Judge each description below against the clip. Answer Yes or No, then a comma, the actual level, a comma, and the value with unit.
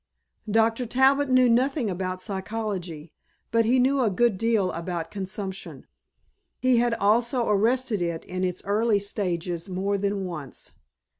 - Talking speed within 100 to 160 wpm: Yes, average, 140 wpm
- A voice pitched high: Yes, high, 205 Hz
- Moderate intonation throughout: Yes, average, 4.3 semitones